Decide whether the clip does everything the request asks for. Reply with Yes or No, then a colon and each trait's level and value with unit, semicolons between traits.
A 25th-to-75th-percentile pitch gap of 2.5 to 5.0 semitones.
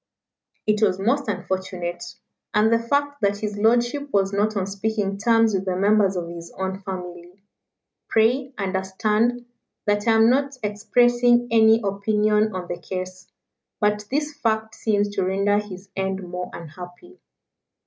Yes: average, 3.1 semitones